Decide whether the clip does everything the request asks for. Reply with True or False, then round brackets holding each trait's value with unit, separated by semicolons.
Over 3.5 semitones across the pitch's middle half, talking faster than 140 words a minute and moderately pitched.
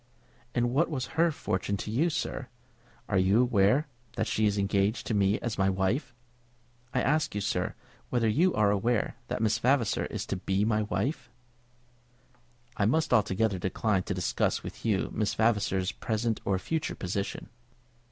False (4.0 semitones; 165 wpm; 110 Hz)